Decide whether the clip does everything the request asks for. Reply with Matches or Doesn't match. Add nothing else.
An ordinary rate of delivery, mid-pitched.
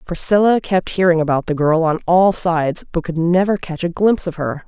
Doesn't match